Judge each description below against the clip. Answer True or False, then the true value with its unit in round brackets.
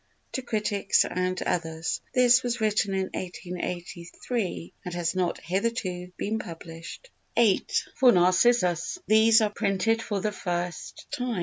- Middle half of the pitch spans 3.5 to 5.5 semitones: True (4.1 semitones)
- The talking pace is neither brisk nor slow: False (130 wpm)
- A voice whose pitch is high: True (195 Hz)